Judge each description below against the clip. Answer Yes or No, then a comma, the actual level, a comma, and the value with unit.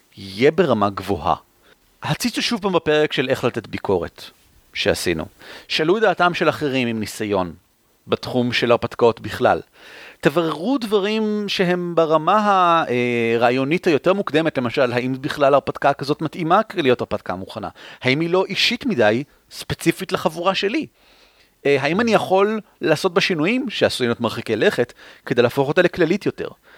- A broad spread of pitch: Yes, wide, 7.7 semitones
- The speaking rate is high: No, average, 140 wpm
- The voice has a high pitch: No, medium, 150 Hz